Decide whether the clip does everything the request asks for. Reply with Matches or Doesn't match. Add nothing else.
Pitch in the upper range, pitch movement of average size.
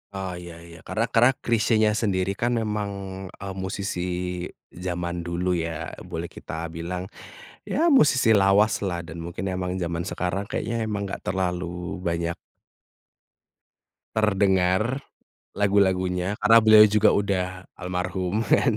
Doesn't match